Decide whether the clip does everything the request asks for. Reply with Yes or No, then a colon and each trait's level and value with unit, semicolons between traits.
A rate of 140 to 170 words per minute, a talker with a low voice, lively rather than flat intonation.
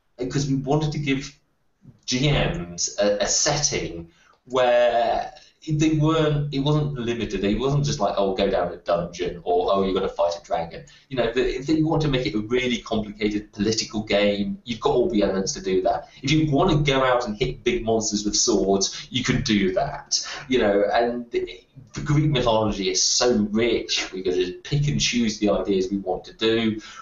No: average, 200 wpm; low, 115 Hz; wide, 5.7 semitones